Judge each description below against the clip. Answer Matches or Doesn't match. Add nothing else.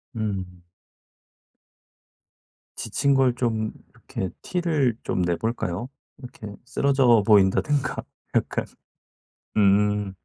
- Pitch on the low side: Matches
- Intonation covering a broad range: Doesn't match